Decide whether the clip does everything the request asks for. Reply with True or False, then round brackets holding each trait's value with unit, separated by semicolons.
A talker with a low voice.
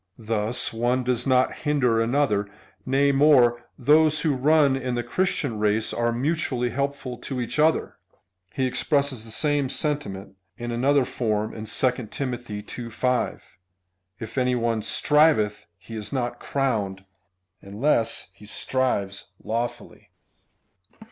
True (125 Hz)